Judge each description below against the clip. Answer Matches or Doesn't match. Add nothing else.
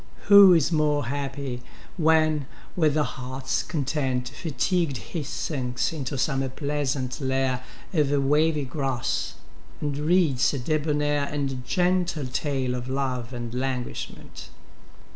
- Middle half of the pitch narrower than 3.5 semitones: Matches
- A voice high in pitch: Doesn't match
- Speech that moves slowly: Matches